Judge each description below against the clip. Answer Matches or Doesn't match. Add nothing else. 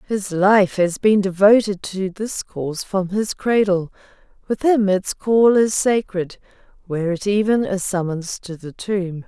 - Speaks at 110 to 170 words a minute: Matches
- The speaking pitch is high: Matches